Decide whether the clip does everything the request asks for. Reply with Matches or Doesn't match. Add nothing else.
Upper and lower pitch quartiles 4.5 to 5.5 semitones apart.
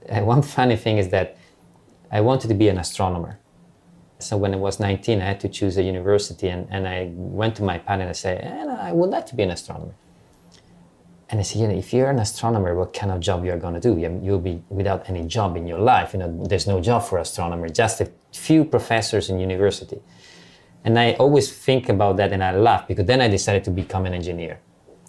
Doesn't match